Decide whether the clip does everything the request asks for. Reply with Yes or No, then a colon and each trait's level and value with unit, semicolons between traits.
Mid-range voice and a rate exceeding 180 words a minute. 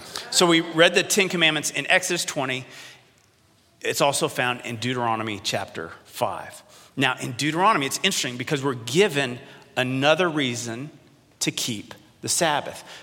No: medium, 145 Hz; average, 140 wpm